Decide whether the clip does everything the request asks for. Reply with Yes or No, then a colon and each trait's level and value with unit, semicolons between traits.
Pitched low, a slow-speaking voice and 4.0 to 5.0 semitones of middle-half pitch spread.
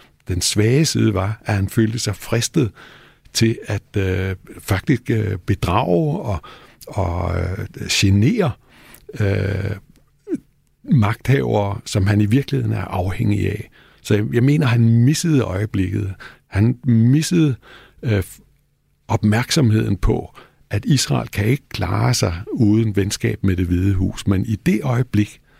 No: low, 105 Hz; slow, 125 wpm; average, 3.4 semitones